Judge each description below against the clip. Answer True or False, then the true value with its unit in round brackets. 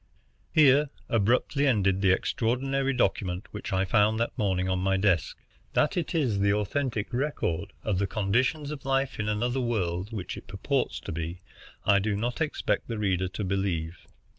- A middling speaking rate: True (170 wpm)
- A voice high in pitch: False (105 Hz)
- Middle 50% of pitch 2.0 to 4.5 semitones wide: False (5.2 semitones)